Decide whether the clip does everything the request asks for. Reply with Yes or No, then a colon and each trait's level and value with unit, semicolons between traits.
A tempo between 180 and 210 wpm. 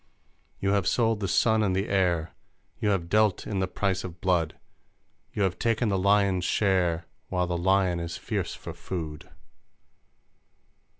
No: average, 160 wpm